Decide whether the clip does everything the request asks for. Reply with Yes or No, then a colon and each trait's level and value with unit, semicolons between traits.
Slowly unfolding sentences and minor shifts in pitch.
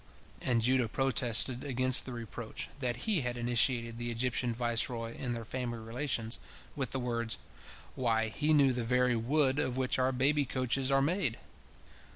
No: average, 165 wpm; narrow, 2.1 semitones